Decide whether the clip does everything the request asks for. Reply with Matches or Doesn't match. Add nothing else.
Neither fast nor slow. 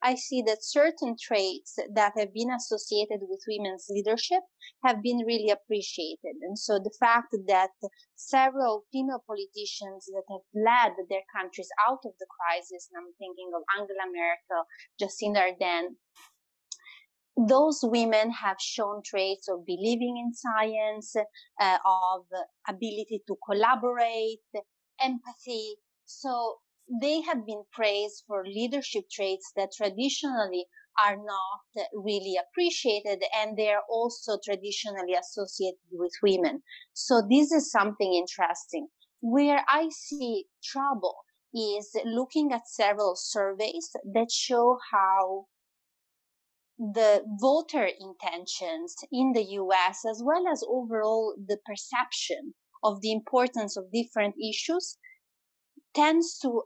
Doesn't match